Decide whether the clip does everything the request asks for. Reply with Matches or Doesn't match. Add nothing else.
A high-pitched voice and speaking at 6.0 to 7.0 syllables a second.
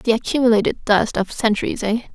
Matches